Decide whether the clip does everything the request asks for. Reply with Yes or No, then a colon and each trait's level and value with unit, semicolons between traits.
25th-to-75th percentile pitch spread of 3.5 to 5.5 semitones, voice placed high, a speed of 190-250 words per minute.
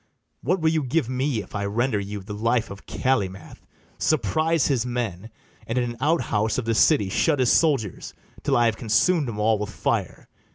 No: average, 5.1 semitones; low, 120 Hz; average, 200 wpm